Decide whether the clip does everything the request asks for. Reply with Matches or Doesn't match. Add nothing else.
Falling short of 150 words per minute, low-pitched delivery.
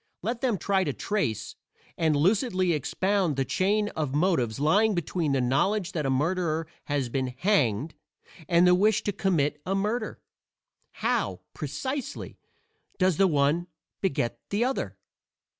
Doesn't match